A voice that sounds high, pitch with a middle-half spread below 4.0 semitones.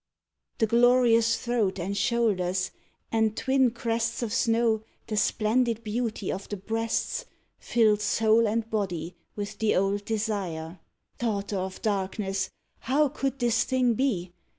Yes: high, 220 Hz; average, 2.9 semitones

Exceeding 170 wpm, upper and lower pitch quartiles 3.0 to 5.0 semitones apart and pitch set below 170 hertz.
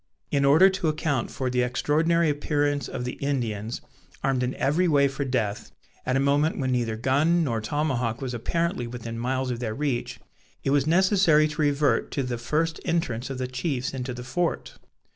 Yes: average, 185 wpm; average, 3.7 semitones; low, 135 Hz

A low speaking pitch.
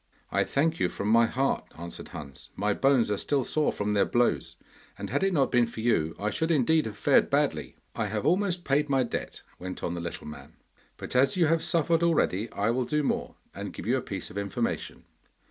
Yes: low, 120 Hz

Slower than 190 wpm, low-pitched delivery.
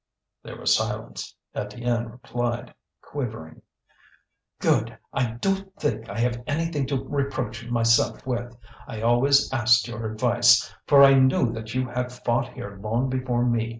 Yes: average, 145 wpm; low, 120 Hz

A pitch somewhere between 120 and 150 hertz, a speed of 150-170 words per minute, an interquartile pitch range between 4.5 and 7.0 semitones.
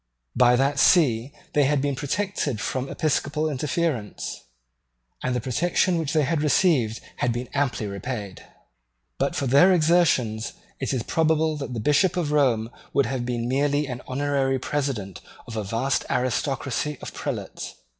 No: low, 135 Hz; average, 155 wpm; average, 3.6 semitones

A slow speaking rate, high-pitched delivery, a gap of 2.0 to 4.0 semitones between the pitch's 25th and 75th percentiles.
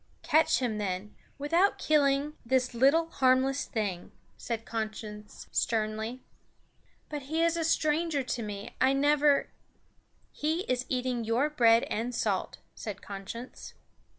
No: slow, 130 wpm; very high, 255 Hz; average, 5.0 semitones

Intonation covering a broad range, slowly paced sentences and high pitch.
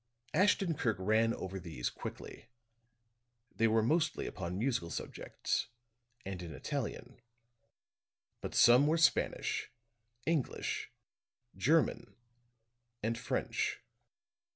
No: wide, 7.6 semitones; slow, 95 wpm; low, 115 Hz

